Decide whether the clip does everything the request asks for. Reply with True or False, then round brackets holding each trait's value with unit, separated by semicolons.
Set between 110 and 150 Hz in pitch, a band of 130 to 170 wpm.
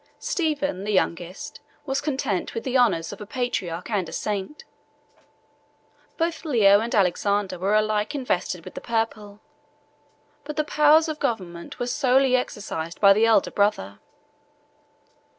False (215 Hz; 140 wpm)